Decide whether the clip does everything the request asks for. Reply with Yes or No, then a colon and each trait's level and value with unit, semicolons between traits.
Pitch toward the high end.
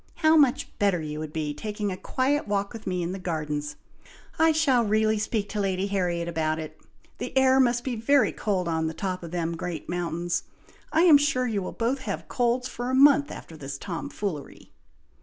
Yes: high, 200 Hz